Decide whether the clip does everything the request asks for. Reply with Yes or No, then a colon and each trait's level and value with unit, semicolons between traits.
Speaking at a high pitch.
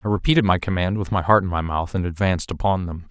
No: very low, 95 Hz